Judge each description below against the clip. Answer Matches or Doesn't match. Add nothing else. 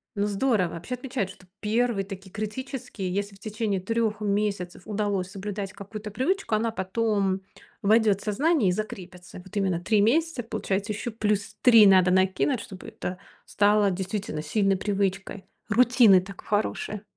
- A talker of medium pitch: Doesn't match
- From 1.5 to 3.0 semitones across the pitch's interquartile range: Matches